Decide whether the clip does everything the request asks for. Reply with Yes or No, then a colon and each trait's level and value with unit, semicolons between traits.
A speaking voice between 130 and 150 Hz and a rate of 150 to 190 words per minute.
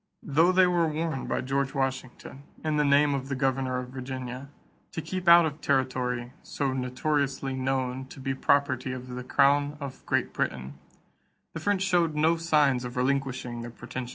Yes: low, 135 Hz; average, 175 wpm